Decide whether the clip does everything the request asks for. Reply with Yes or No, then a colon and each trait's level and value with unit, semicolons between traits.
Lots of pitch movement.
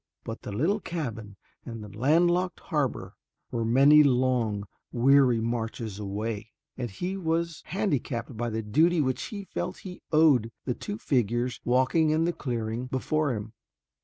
Yes: wide, 5.8 semitones